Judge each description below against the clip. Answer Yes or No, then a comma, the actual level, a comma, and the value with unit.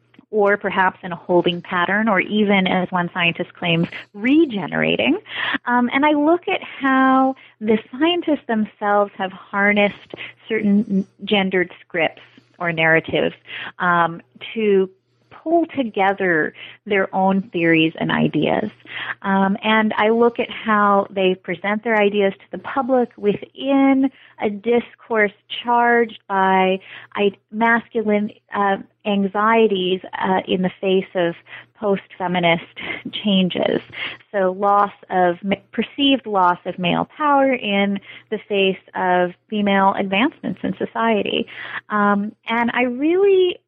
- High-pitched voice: Yes, high, 205 Hz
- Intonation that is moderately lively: Yes, average, 3.8 semitones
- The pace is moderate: No, slow, 120 wpm